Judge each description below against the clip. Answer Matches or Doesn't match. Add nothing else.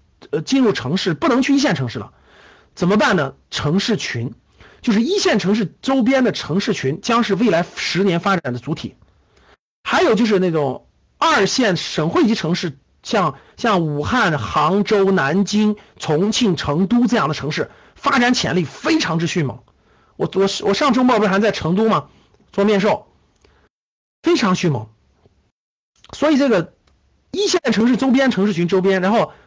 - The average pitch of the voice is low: Doesn't match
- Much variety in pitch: Matches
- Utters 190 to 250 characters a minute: Matches